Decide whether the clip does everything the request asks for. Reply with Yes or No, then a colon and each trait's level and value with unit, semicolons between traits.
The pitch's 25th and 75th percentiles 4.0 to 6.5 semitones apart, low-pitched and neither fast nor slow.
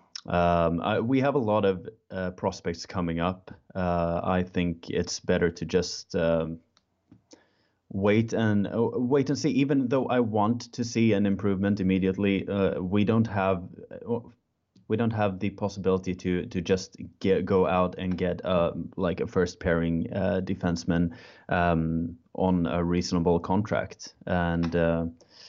No: average, 3.1 semitones; very low, 95 Hz; average, 155 wpm